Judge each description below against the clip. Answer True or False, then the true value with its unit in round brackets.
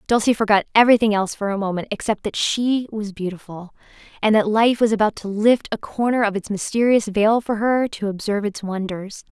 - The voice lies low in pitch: False (215 Hz)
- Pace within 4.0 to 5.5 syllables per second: False (5.7 syllables/s)